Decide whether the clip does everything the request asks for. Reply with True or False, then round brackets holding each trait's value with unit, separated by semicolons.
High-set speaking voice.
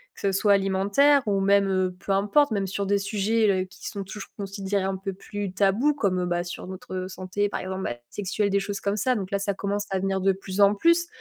True (200 Hz)